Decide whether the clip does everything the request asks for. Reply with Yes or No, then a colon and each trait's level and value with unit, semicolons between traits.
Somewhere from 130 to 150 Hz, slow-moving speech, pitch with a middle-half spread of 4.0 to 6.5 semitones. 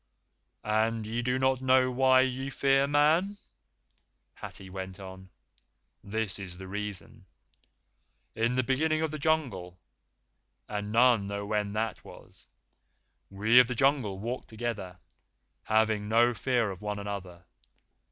No: low, 110 Hz; slow, 130 wpm; average, 4.4 semitones